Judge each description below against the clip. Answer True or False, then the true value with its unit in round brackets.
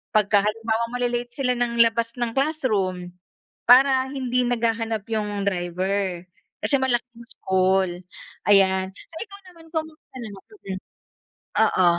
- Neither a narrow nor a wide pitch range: True (4.5 semitones)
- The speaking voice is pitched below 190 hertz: False (230 Hz)